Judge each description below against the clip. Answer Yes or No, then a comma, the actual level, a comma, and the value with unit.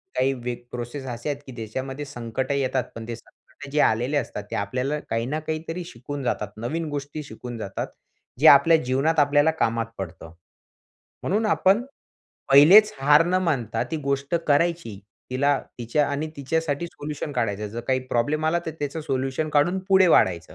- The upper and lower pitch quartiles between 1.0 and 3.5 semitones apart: No, average, 4.2 semitones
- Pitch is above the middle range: No, medium, 140 Hz